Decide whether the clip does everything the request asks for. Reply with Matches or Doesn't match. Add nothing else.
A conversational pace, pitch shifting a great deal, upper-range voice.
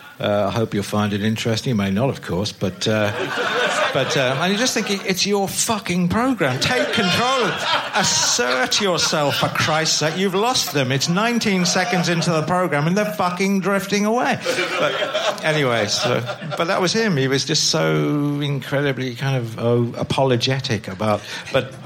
Doesn't match